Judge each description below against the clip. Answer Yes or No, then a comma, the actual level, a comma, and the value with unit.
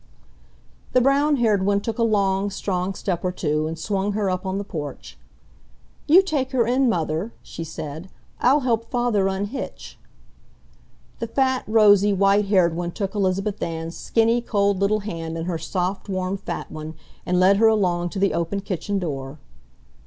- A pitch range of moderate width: Yes, average, 3.8 semitones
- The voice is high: Yes, high, 195 Hz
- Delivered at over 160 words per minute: Yes, average, 170 wpm